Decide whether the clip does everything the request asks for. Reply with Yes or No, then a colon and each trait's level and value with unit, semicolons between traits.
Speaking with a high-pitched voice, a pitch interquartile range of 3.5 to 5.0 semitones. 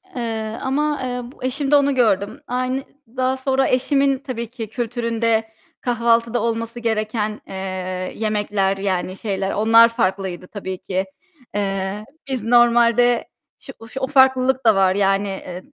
Yes: high, 230 Hz; average, 3.8 semitones